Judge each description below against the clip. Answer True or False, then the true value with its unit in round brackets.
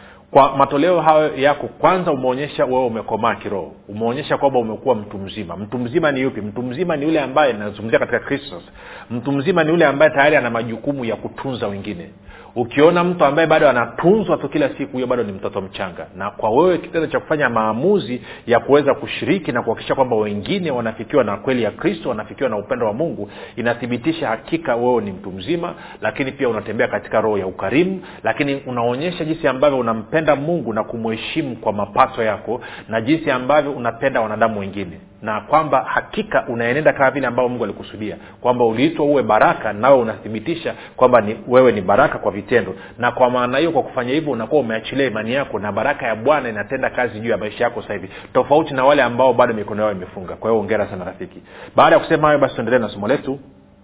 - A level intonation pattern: False (5.0 semitones)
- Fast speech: True (190 wpm)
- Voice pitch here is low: True (125 Hz)